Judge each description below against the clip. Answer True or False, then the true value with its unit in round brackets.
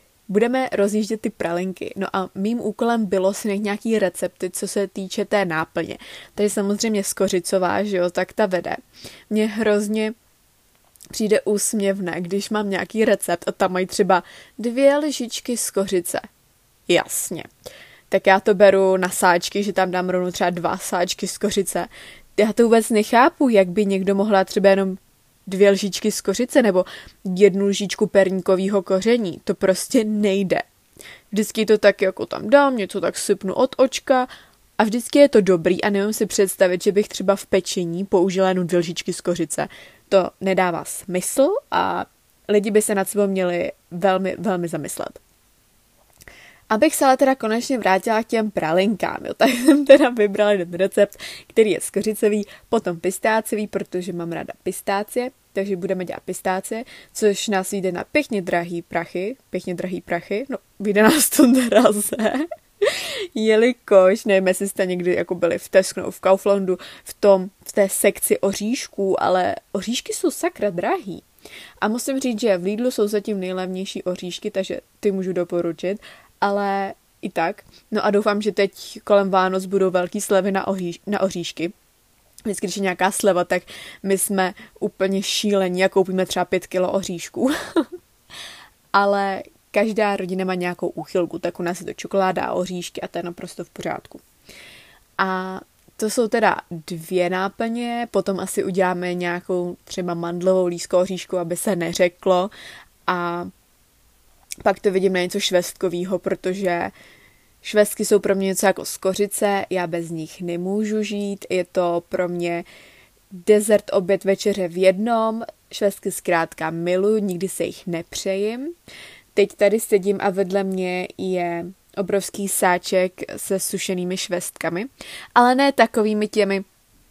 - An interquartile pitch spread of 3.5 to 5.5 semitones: False (2.5 semitones)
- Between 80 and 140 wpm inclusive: False (150 wpm)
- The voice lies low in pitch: False (195 Hz)